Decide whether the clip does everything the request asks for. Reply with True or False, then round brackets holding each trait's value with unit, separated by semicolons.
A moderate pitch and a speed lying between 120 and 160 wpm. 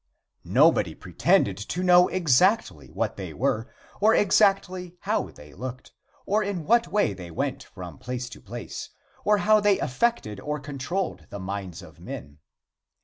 True (150 Hz; 150 wpm)